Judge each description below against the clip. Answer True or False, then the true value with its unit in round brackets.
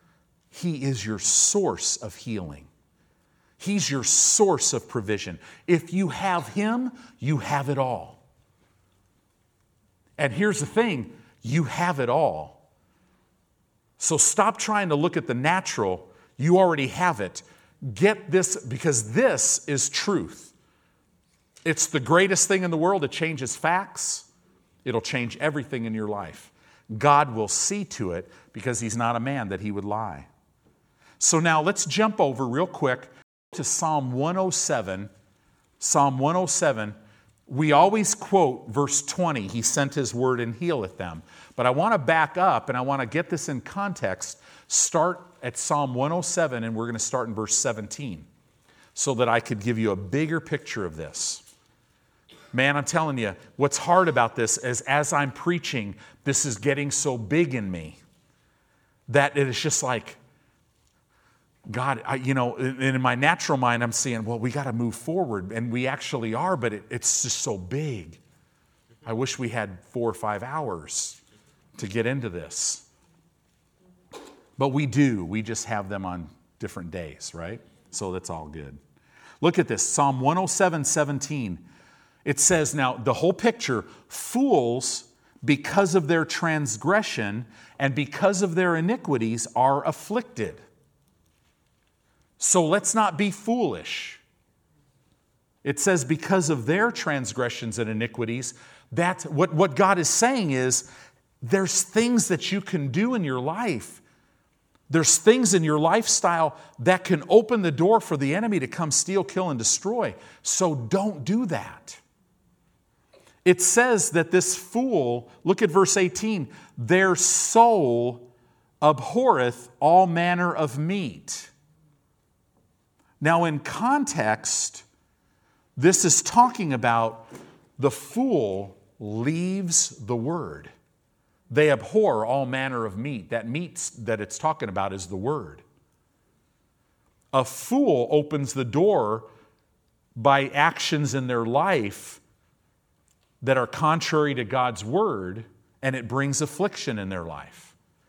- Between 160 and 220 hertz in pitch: False (140 Hz)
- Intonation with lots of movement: True (6.9 semitones)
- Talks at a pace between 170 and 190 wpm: False (145 wpm)